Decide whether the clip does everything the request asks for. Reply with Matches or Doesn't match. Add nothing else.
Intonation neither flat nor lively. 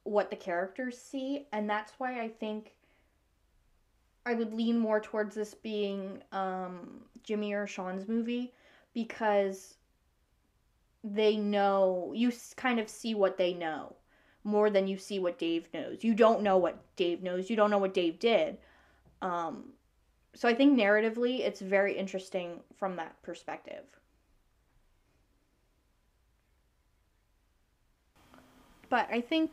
Matches